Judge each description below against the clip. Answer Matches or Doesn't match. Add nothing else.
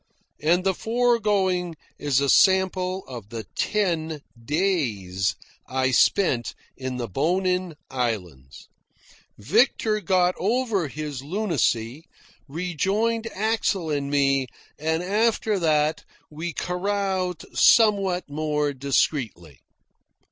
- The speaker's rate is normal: Doesn't match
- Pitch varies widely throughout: Matches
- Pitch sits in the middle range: Matches